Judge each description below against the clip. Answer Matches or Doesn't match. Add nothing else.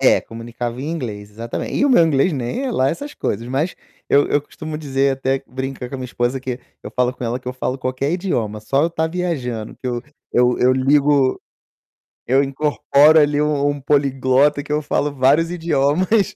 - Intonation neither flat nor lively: Matches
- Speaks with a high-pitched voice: Doesn't match